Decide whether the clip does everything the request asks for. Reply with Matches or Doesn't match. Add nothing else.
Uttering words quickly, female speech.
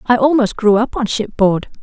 Doesn't match